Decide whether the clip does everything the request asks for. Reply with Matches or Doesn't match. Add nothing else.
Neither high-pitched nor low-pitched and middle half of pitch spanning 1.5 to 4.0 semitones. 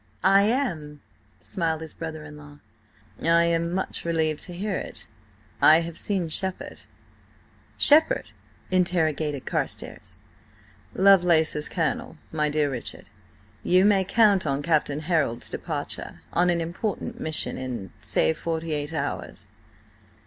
Matches